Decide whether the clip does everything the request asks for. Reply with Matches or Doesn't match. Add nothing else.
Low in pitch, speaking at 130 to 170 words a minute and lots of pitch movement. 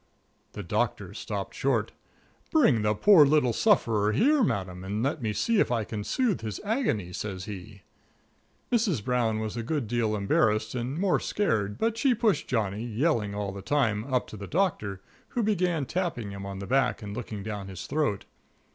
Doesn't match